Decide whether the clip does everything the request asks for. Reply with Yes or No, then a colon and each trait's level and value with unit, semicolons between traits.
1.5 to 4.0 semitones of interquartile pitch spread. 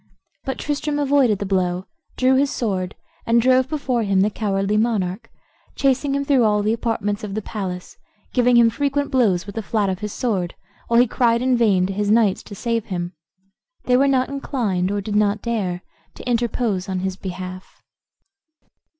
No: average, 4.4 semitones